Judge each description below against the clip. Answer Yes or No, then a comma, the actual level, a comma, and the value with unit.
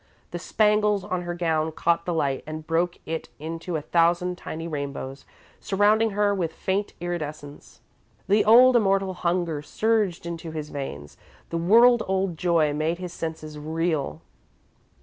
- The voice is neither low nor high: Yes, medium, 170 Hz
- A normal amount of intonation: Yes, average, 3.6 semitones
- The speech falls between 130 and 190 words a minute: Yes, average, 150 wpm